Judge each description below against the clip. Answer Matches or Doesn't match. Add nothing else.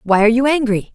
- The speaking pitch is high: Matches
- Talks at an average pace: Doesn't match